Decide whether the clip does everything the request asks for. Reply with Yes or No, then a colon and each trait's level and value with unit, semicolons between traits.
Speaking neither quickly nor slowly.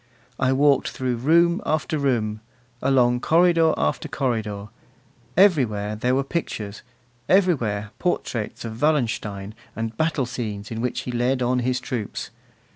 No: slow, 130 wpm